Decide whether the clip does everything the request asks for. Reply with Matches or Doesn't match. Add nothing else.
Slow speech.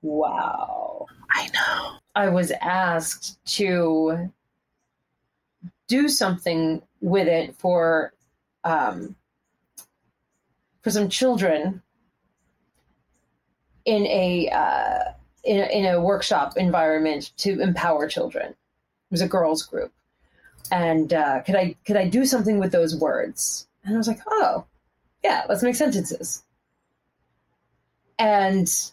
Matches